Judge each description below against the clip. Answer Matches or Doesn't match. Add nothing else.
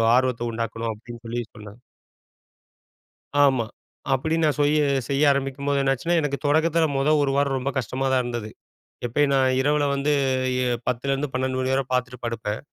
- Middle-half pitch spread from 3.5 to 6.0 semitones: Doesn't match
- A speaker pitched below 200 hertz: Matches